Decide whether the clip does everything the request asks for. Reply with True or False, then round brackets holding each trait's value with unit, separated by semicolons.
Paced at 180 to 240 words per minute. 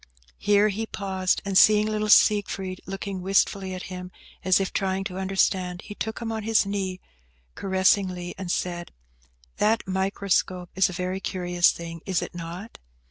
False (160 wpm)